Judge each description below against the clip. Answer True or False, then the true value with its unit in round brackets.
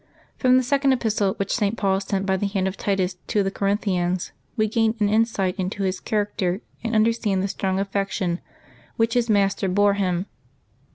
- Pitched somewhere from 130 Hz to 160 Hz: False (200 Hz)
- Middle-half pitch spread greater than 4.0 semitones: False (2.4 semitones)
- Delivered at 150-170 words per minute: False (185 wpm)